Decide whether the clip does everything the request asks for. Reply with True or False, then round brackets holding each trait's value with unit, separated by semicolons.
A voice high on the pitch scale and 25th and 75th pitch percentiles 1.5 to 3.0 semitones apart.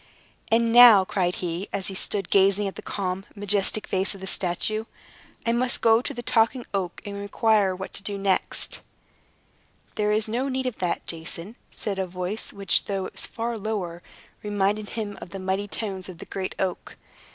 True (200 Hz; 2.5 semitones)